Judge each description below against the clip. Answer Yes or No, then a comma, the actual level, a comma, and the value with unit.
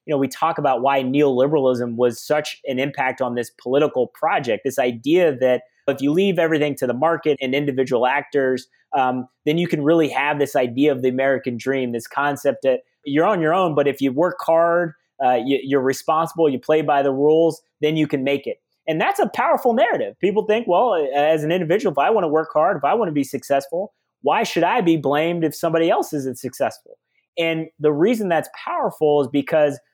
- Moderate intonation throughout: Yes, average, 3.3 semitones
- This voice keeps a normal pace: No, fast, 210 wpm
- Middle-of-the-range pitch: Yes, medium, 150 Hz